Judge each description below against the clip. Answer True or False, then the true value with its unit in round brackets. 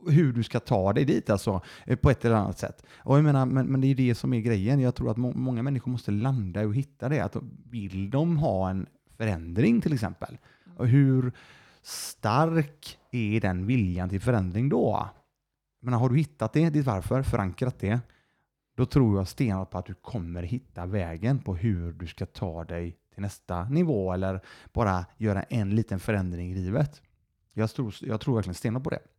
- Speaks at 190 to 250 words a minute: True (195 wpm)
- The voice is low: True (115 Hz)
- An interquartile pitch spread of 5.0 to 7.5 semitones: True (5.4 semitones)